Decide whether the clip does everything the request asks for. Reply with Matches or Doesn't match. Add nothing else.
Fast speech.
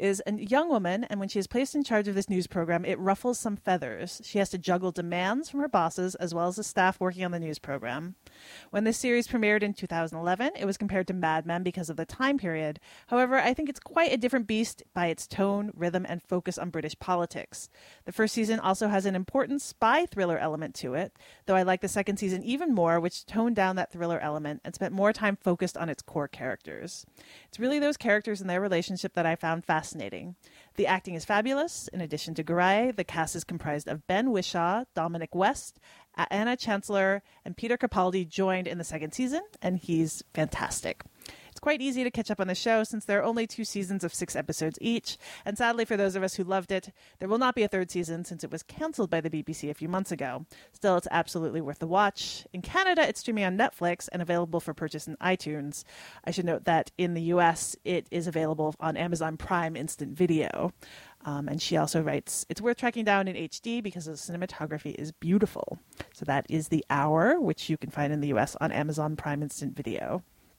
Matches